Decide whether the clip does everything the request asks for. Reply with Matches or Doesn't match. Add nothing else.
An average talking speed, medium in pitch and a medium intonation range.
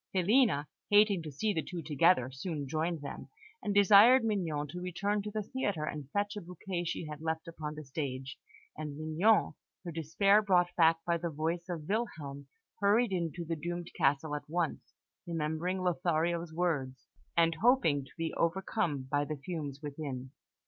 Matches